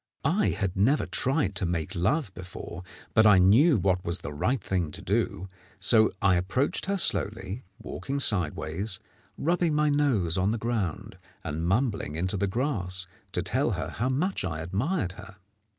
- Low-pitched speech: Yes, low, 100 Hz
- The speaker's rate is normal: Yes, average, 170 wpm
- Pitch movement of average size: No, wide, 6.4 semitones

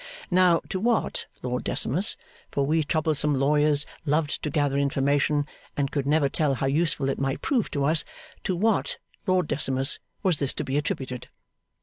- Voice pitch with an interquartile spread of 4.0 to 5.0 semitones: No, average, 2.8 semitones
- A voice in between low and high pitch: Yes, medium, 145 Hz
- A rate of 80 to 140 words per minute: No, average, 165 wpm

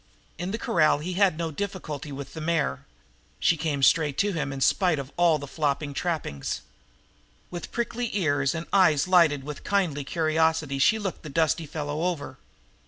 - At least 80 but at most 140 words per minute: No, average, 170 wpm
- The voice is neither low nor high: Yes, medium, 160 Hz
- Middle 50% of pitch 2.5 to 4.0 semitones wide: Yes, average, 3.5 semitones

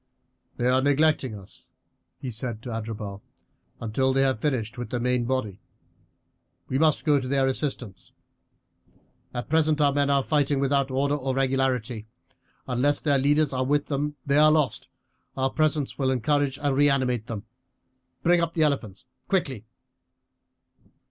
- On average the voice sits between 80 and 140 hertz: Yes, low, 135 Hz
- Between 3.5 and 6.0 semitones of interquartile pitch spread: No, average, 2.9 semitones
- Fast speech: No, average, 150 wpm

